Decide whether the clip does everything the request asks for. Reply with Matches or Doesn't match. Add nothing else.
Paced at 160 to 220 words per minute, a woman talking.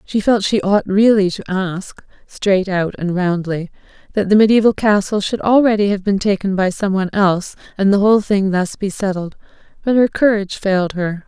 Matches